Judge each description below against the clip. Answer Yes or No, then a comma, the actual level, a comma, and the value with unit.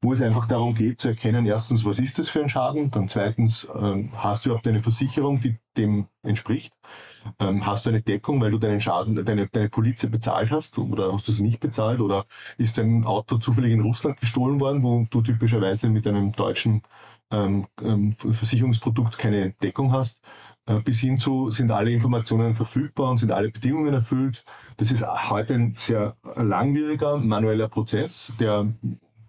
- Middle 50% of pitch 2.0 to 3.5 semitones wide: Yes, average, 2.8 semitones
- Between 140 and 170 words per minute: No, average, 180 wpm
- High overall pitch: No, low, 115 Hz